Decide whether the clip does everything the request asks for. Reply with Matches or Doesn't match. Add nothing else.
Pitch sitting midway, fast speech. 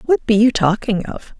Doesn't match